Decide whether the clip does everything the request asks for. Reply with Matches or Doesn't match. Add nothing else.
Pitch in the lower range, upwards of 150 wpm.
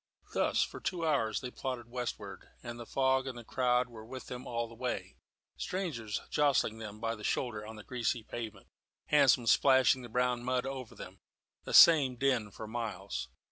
Matches